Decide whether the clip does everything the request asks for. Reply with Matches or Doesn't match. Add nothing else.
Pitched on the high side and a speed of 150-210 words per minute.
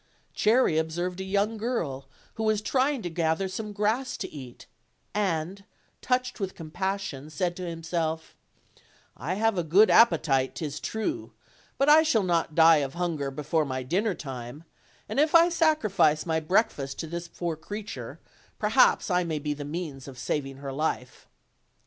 Doesn't match